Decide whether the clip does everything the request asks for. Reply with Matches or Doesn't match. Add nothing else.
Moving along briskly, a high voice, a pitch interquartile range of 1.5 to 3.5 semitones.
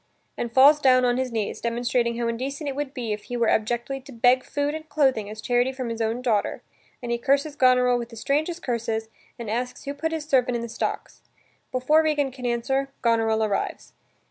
Matches